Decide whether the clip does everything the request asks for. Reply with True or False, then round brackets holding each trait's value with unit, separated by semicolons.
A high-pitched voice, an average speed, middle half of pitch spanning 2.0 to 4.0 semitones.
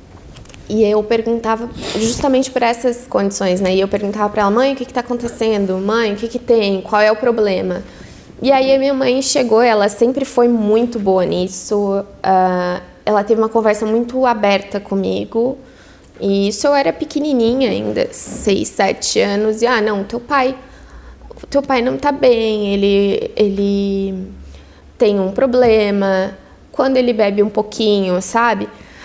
True (220 Hz; 160 wpm; 3.7 semitones)